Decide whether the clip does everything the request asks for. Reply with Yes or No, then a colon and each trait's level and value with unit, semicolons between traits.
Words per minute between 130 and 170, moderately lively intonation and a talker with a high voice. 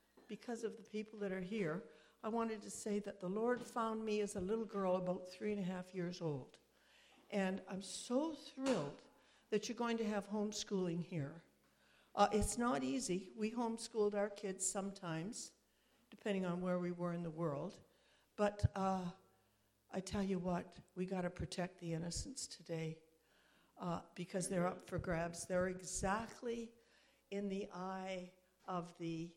Yes: average, 165 wpm; average, 3.5 semitones; high, 195 Hz